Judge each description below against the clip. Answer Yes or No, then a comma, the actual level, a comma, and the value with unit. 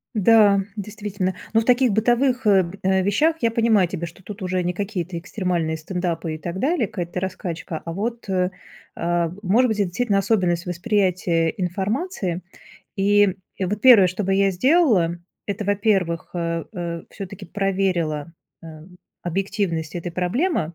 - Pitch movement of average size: Yes, average, 3.4 semitones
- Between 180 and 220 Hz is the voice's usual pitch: Yes, high, 190 Hz